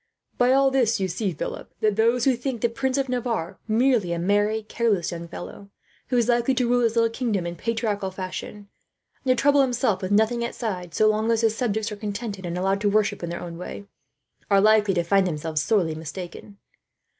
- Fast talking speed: Yes, fast, 210 wpm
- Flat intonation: No, average, 4.0 semitones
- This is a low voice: No, high, 215 Hz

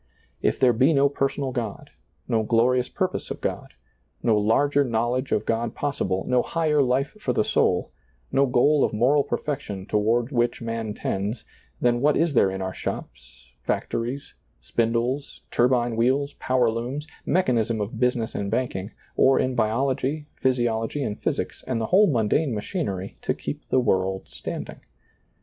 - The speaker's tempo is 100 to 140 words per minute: No, average, 160 wpm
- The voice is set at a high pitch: No, low, 120 Hz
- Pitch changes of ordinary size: Yes, average, 3.7 semitones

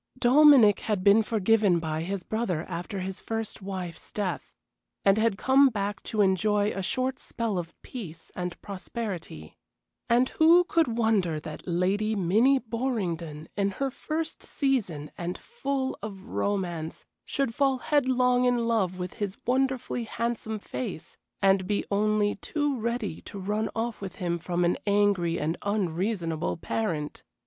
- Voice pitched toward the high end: Yes, high, 205 Hz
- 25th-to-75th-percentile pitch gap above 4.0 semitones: Yes, average, 4.7 semitones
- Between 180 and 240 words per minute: No, average, 145 wpm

